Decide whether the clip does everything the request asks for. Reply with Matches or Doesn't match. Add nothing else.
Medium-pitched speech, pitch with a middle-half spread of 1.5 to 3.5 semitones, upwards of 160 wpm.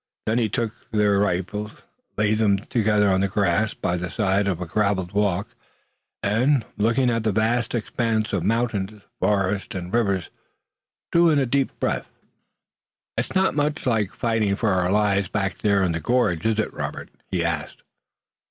Doesn't match